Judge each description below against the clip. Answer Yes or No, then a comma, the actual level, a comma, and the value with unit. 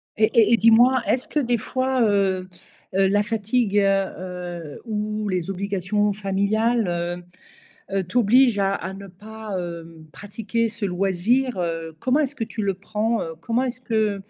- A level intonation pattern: No, average, 3.2 semitones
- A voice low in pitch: No, high, 205 Hz